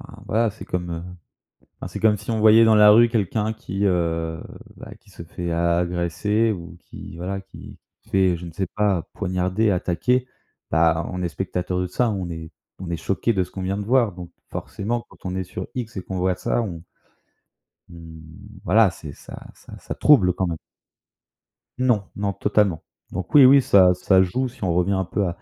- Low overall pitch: Yes, very low, 95 Hz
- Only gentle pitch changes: No, average, 3.5 semitones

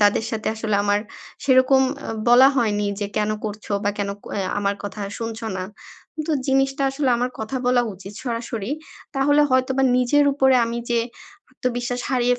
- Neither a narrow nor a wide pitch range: Yes, average, 3.6 semitones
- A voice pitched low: No, high, 240 Hz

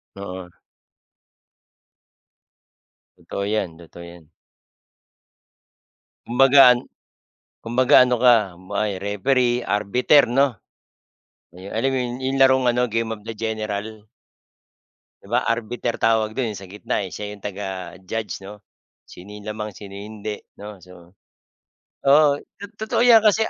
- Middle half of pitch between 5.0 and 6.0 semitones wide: No, average, 3.8 semitones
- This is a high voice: No, low, 110 Hz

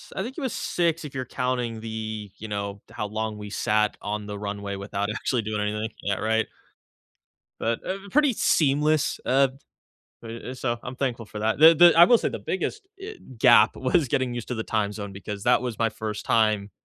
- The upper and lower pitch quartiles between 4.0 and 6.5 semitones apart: Yes, average, 4.3 semitones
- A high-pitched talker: No, low, 115 Hz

